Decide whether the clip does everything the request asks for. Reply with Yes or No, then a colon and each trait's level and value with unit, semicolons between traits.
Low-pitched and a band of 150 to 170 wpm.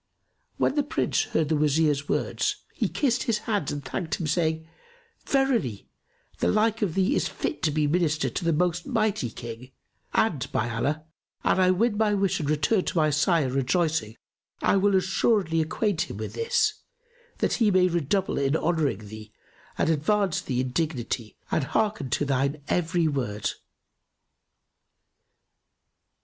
No: medium, 160 Hz; average, 160 wpm